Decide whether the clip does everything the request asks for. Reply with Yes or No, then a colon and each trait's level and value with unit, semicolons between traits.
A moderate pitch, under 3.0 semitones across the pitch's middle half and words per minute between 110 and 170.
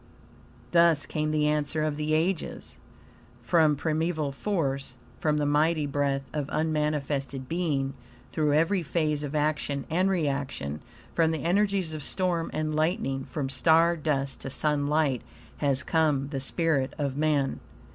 Yes: medium, 150 Hz; narrow, 2.4 semitones; average, 140 wpm